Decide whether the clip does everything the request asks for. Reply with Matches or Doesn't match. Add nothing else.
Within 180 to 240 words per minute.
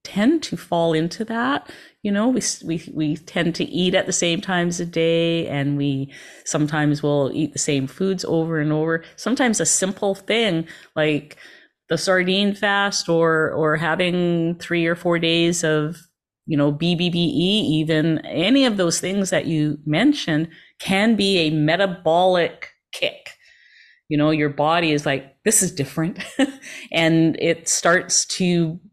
Doesn't match